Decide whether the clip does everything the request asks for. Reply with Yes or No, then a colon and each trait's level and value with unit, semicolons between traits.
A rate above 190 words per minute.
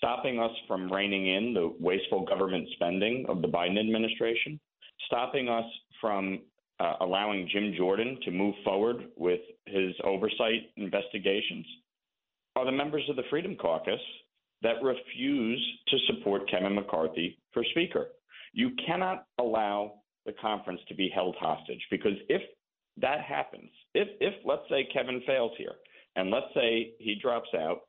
No: average, 145 wpm